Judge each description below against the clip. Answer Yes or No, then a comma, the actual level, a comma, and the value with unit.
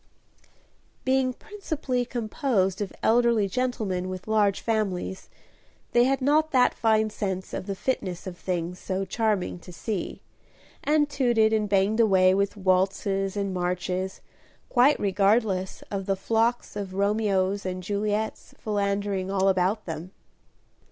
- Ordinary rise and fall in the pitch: Yes, average, 3.2 semitones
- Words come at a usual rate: No, slow, 130 wpm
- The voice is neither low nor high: No, high, 200 Hz